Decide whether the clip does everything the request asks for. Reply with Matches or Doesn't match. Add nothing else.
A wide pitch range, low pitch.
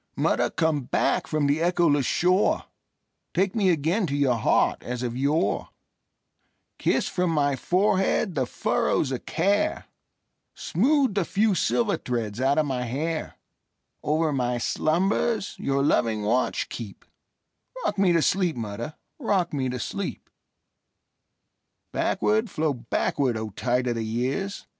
Doesn't match